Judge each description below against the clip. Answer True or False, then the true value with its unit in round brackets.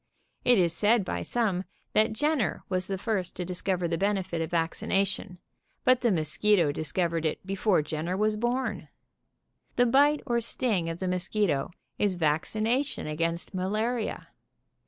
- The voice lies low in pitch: False (190 Hz)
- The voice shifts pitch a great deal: False (4.5 semitones)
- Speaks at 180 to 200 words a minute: False (155 wpm)